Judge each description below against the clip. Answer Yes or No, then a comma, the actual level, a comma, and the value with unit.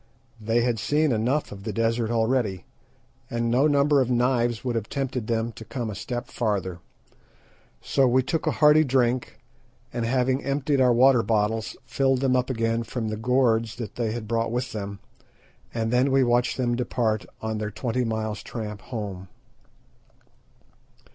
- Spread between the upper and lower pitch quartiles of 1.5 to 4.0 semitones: Yes, narrow, 2.5 semitones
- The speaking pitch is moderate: No, low, 120 Hz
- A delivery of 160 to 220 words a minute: Yes, average, 165 wpm